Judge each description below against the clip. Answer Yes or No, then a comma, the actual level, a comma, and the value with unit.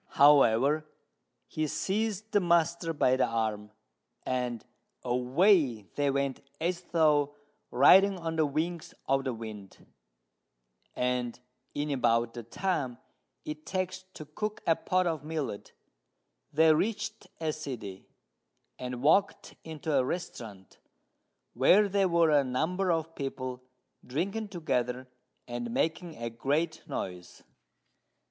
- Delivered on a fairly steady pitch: No, wide, 5.4 semitones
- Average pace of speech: No, slow, 120 wpm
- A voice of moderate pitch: Yes, medium, 150 Hz